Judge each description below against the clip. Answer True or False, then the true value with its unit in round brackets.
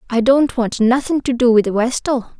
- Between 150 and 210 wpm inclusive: True (200 wpm)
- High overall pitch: True (245 Hz)